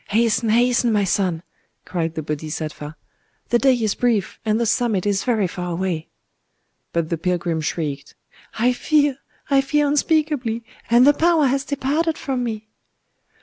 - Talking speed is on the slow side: No, average, 145 wpm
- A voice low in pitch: No, high, 225 Hz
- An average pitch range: No, wide, 7.0 semitones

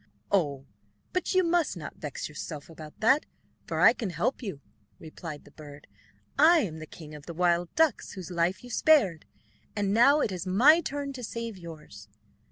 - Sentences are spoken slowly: No, average, 175 wpm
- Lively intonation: Yes, wide, 8.6 semitones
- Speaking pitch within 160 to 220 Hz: Yes, medium, 185 Hz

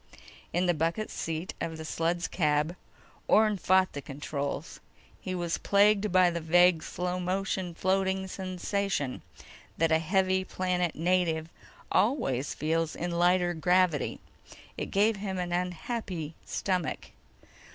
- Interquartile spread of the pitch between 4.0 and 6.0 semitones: No, narrow, 2.5 semitones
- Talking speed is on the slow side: Yes, slow, 130 wpm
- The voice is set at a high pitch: No, medium, 180 Hz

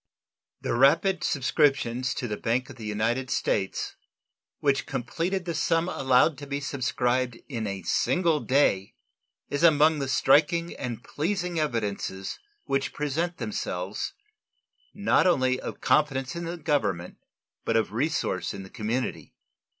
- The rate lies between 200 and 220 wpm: No, slow, 135 wpm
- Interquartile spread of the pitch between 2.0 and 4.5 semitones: No, average, 5.1 semitones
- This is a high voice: No, low, 135 Hz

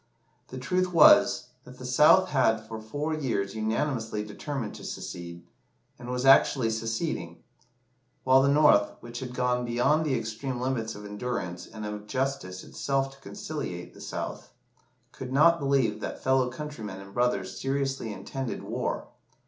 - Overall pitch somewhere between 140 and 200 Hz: No, low, 125 Hz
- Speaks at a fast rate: No, average, 150 wpm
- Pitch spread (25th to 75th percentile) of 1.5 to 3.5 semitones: No, average, 3.9 semitones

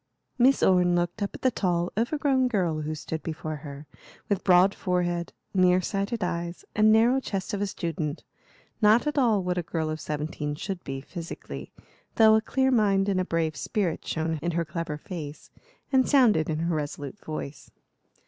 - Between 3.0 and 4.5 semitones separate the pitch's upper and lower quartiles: No, average, 4.9 semitones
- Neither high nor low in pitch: Yes, medium, 180 Hz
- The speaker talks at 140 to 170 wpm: No, average, 180 wpm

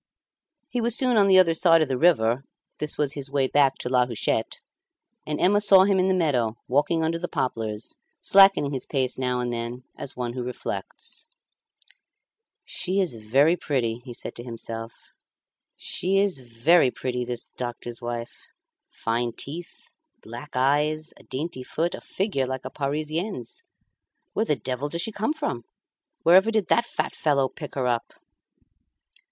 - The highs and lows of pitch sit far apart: Yes, wide, 6.0 semitones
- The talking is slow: No, average, 165 wpm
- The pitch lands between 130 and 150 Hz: Yes, medium, 140 Hz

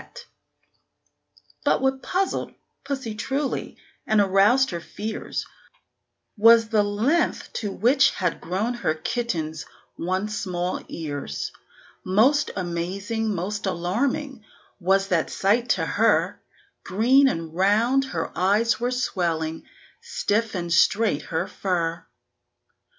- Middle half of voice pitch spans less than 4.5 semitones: No, average, 5.3 semitones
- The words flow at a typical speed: No, slow, 110 wpm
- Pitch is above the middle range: Yes, high, 205 Hz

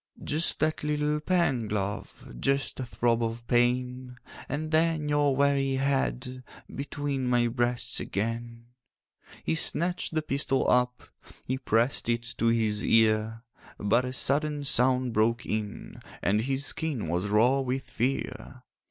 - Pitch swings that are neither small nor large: Yes, average, 3.4 semitones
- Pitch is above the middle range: No, low, 125 Hz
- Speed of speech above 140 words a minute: No, slow, 135 wpm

